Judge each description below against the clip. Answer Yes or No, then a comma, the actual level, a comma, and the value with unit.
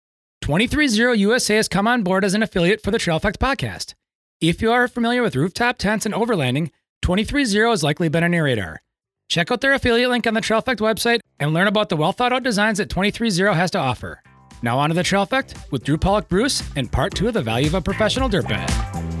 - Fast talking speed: Yes, fast, 240 wpm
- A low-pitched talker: No, high, 200 Hz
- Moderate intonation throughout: No, wide, 6.7 semitones